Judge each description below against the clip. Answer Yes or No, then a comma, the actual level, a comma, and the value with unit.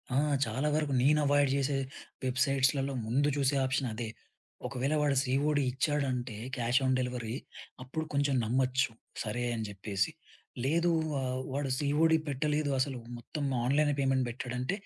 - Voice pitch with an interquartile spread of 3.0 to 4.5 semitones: No, narrow, 2.4 semitones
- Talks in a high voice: No, low, 135 Hz